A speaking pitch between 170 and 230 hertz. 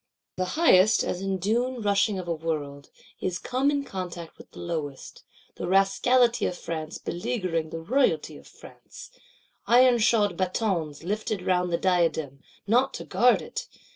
Yes: medium, 185 Hz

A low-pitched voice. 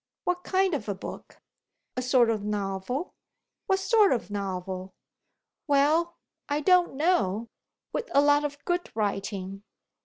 No: very high, 265 Hz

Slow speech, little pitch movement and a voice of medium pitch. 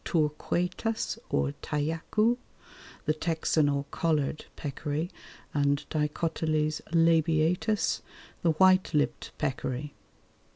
Yes: slow, 85 wpm; narrow, 2.2 semitones; medium, 155 Hz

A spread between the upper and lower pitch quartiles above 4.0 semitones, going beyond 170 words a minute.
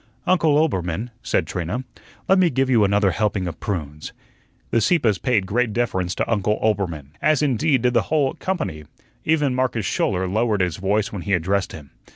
Yes: wide, 5.6 semitones; average, 180 wpm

